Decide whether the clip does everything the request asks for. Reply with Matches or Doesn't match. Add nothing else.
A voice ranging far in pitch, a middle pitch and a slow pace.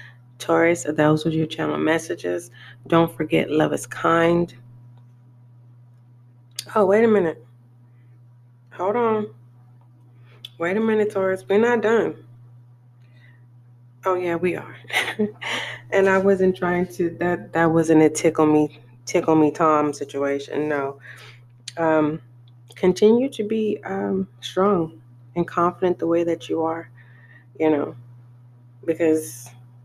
Matches